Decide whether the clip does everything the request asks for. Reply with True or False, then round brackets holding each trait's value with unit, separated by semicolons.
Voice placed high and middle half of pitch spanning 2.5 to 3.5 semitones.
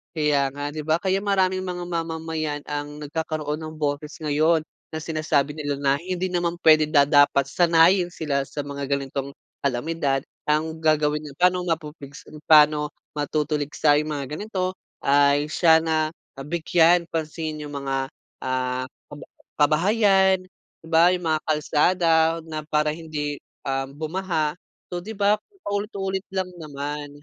False (155 Hz; 2.8 semitones)